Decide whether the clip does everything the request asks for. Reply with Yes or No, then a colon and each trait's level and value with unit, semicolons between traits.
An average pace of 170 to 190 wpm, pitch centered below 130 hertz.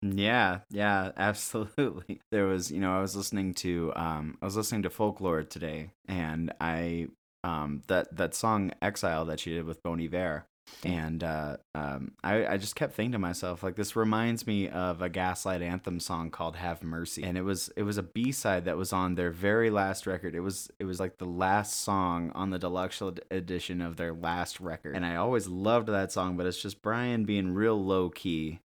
No: fast, 205 wpm; very low, 90 Hz